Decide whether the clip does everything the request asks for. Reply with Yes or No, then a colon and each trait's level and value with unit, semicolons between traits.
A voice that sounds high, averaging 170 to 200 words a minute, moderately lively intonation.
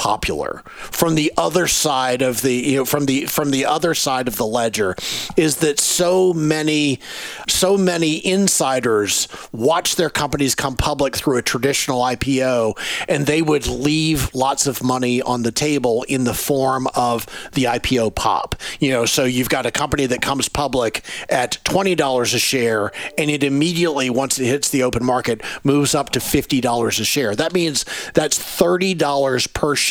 No: medium, 140 Hz; average, 180 wpm; average, 3.6 semitones